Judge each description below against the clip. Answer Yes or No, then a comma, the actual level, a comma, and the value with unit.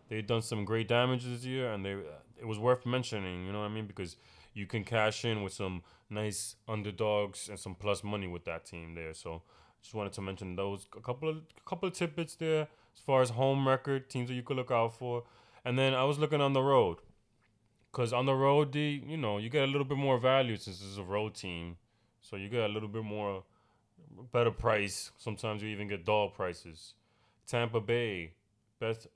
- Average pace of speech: No, fast, 220 wpm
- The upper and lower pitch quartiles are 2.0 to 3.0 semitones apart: No, average, 3.8 semitones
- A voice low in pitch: Yes, low, 110 Hz